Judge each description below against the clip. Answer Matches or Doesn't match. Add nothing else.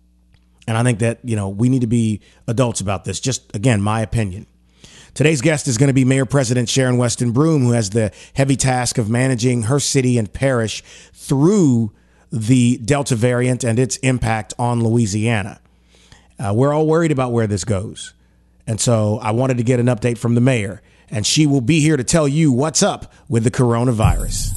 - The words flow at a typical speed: Matches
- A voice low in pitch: Matches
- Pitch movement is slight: Doesn't match